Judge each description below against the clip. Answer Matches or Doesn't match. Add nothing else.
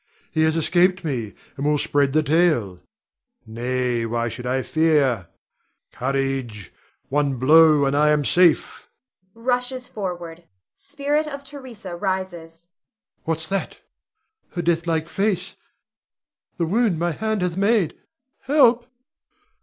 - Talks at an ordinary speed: Doesn't match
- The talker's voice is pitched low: Doesn't match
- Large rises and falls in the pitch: Matches